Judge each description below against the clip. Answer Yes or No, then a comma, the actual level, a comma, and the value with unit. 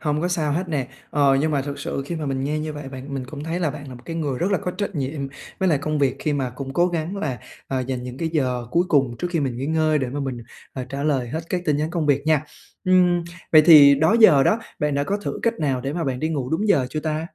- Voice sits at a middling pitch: Yes, medium, 150 Hz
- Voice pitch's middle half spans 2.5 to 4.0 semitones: Yes, average, 3.1 semitones